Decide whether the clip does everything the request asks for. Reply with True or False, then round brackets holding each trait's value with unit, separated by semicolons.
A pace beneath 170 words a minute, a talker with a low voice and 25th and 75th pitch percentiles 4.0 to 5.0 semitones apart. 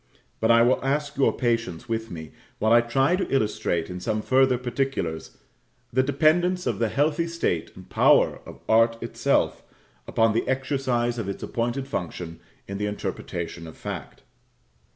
True (160 wpm; 120 Hz; 4.5 semitones)